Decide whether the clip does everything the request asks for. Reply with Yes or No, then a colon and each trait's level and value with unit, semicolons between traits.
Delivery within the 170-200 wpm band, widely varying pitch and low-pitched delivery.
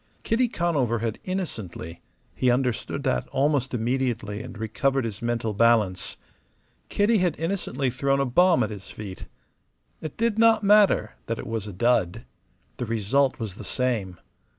No: average, 150 wpm; wide, 6.1 semitones; low, 125 Hz